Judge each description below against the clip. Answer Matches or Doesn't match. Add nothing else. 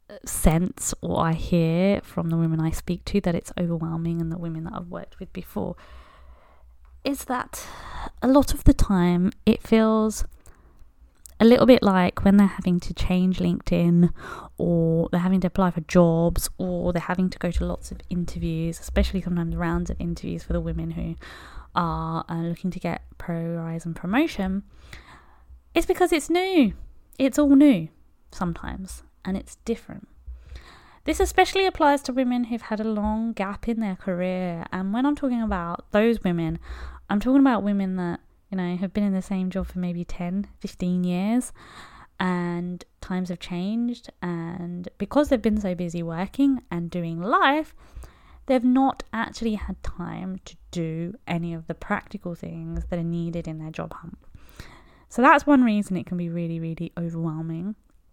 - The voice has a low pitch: Doesn't match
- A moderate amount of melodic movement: Matches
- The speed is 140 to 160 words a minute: Doesn't match